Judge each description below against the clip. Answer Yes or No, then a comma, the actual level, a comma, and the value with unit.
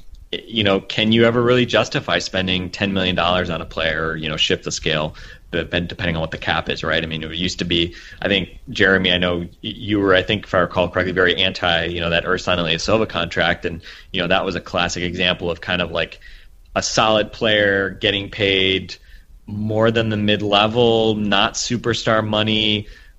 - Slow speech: No, average, 200 wpm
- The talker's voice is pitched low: Yes, very low, 95 Hz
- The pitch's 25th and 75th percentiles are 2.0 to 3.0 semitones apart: No, average, 3.7 semitones